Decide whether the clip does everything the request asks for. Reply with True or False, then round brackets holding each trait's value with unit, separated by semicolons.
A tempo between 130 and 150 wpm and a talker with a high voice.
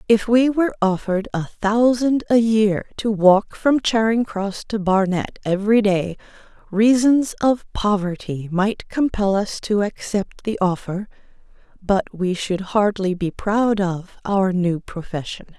True (140 wpm; 205 Hz)